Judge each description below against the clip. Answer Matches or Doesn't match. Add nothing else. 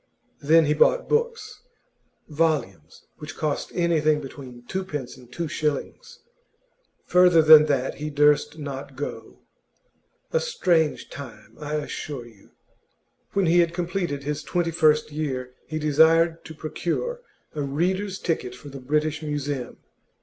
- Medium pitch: Matches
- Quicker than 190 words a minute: Doesn't match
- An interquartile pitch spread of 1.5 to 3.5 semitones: Matches